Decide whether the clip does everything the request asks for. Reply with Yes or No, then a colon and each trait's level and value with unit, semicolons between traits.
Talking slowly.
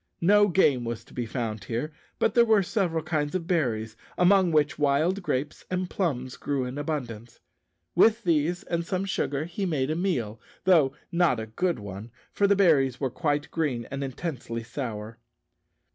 No: average, 175 wpm